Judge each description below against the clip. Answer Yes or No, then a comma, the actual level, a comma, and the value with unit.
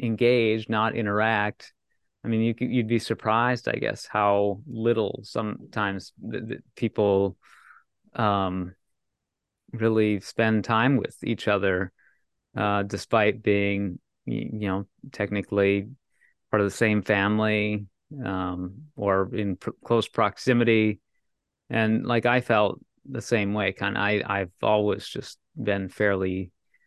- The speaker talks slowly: Yes, slow, 125 wpm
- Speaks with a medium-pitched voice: No, low, 105 Hz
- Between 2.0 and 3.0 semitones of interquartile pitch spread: Yes, narrow, 2.4 semitones